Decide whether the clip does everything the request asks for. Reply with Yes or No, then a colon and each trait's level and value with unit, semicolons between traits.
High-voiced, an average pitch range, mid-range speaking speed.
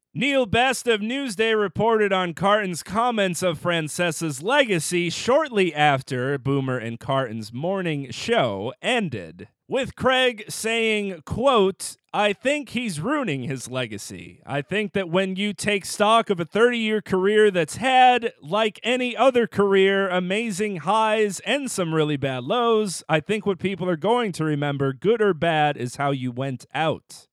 No: high, 195 Hz; wide, 6.3 semitones; average, 150 wpm